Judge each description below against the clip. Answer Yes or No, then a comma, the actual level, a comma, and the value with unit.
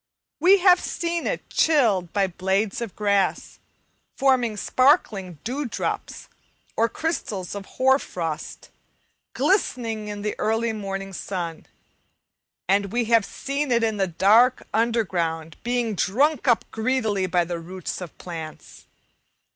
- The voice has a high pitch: Yes, high, 215 Hz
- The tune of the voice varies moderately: Yes, average, 4.8 semitones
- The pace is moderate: No, slow, 130 wpm